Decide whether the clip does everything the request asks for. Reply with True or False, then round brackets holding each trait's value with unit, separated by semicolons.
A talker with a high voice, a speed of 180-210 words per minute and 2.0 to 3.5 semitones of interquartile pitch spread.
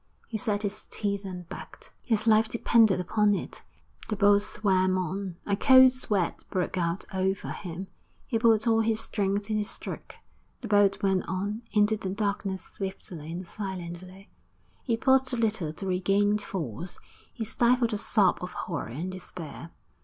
False (200 Hz; 165 wpm; 2.8 semitones)